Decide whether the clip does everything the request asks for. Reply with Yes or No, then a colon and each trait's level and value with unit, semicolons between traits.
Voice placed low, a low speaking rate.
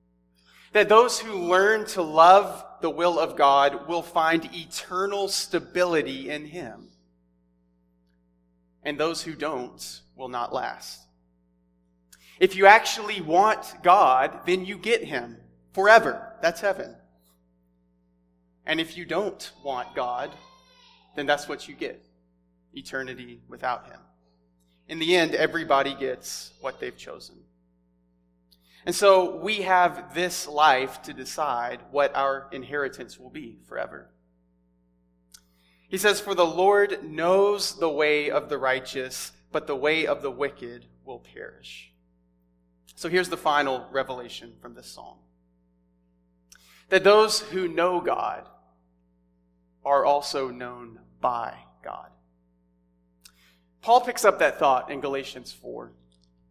Yes: low, 130 Hz; slow, 125 wpm